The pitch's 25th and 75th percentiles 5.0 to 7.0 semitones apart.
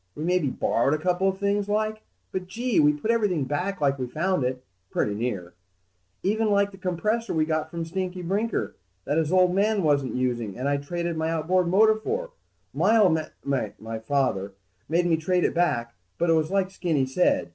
Yes: wide, 5.4 semitones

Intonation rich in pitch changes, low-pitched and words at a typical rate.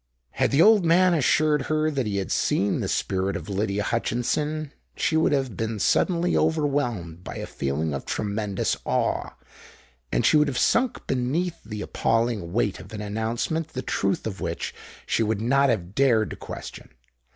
Yes: wide, 7.0 semitones; low, 120 Hz; average, 175 wpm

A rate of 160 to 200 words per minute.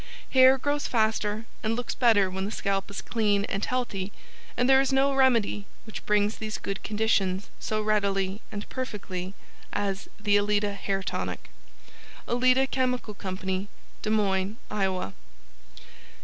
No: average, 140 wpm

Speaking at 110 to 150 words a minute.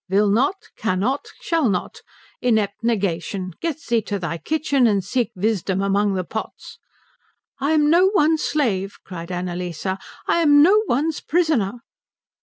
Yes: average, 145 wpm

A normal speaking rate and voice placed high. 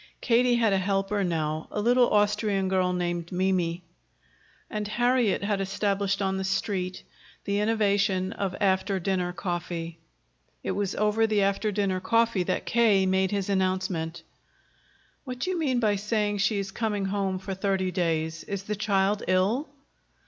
Yes: average, 155 wpm; high, 195 Hz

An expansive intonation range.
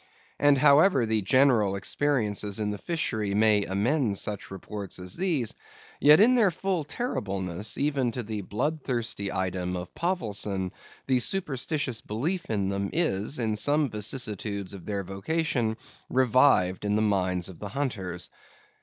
Yes: wide, 6.5 semitones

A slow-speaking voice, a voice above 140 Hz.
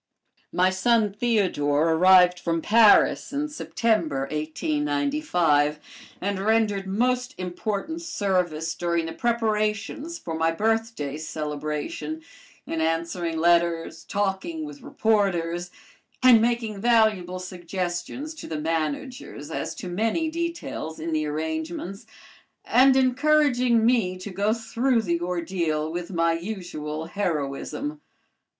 Yes: slow, 110 wpm; high, 190 Hz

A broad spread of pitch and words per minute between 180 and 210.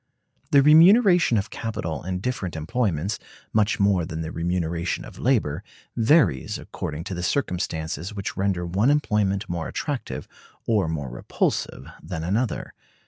No: wide, 5.9 semitones; average, 140 wpm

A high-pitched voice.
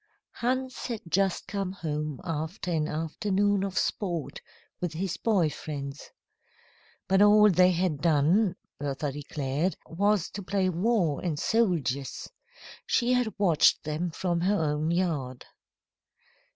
No: medium, 175 Hz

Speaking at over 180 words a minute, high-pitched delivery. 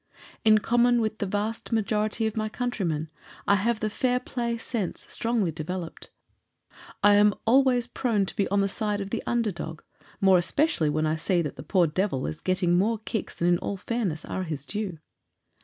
Yes: average, 190 wpm; high, 205 Hz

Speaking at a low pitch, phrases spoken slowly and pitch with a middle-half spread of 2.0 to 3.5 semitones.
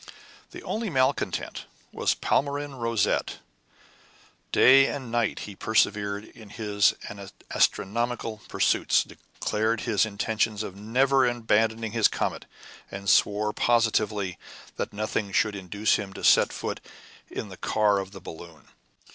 Yes: low, 110 Hz; slow, 125 wpm; narrow, 2.6 semitones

